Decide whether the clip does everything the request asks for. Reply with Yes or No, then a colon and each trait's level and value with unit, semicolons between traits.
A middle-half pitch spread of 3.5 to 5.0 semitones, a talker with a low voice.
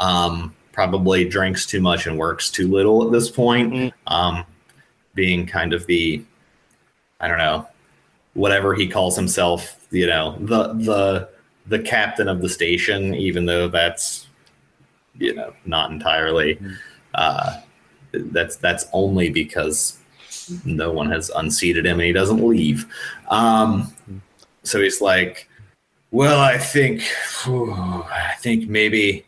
Yes: average, 4.2 semitones; very low, 95 Hz